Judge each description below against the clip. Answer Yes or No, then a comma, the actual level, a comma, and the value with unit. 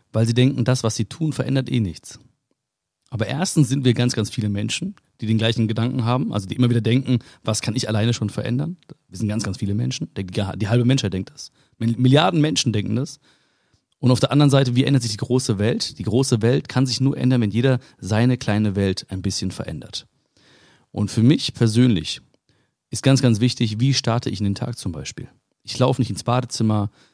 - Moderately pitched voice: No, low, 120 Hz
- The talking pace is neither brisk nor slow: No, fast, 210 wpm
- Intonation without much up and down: No, average, 3.1 semitones